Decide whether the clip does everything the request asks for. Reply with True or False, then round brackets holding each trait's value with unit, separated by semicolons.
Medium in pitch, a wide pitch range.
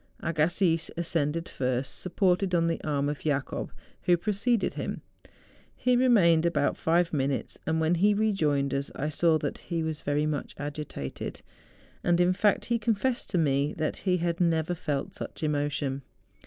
False (165 Hz; 3.6 semitones)